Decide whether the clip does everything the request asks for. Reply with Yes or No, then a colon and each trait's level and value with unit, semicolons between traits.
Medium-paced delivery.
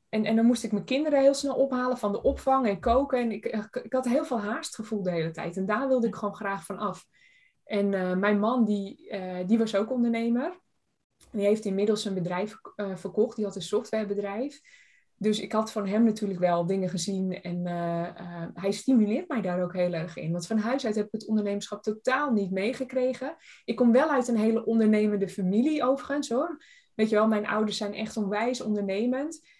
No: fast, 215 wpm